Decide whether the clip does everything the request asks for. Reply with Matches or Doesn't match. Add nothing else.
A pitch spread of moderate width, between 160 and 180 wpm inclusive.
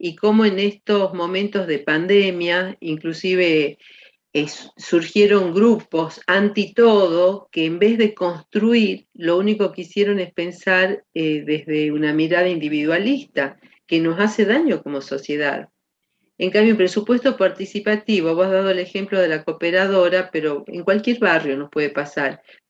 Doesn't match